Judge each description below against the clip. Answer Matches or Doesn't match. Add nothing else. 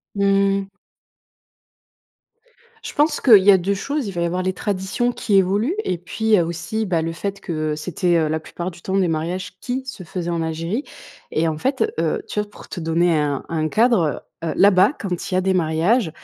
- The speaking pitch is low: Doesn't match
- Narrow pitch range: Doesn't match